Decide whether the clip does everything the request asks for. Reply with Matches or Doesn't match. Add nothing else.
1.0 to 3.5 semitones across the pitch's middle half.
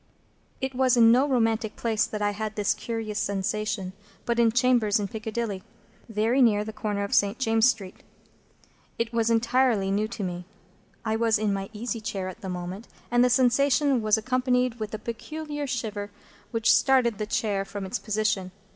Matches